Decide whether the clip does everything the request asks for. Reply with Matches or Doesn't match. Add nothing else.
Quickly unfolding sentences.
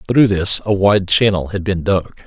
Matches